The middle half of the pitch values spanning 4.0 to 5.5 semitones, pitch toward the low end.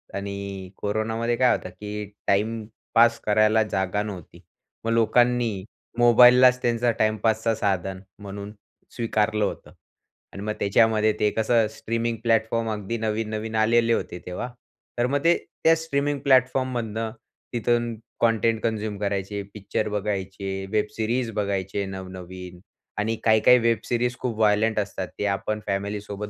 No: narrow, 2.4 semitones; low, 110 Hz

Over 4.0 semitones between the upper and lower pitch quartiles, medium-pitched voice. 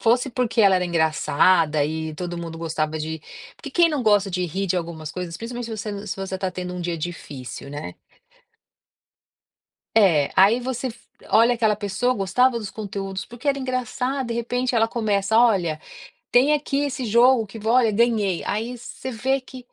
No: wide, 5.6 semitones; high, 210 Hz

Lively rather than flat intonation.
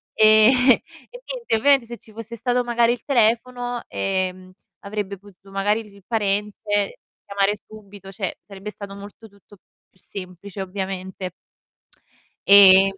No: narrow, 2.6 semitones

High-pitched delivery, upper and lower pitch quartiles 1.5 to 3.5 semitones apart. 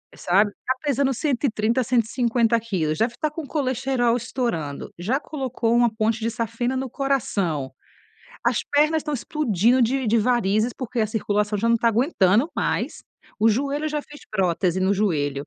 No: high, 230 Hz; average, 4.0 semitones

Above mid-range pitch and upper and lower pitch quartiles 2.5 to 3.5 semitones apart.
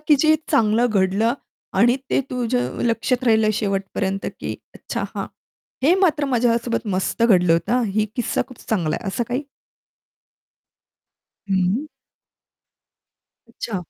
No: high, 230 Hz; average, 4.1 semitones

